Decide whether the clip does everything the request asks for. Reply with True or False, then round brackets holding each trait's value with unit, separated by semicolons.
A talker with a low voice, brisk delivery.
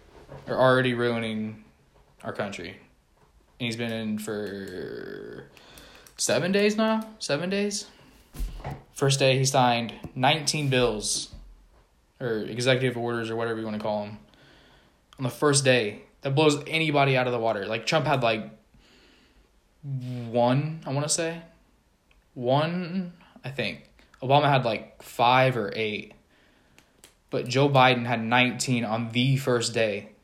False (125 Hz; 135 wpm)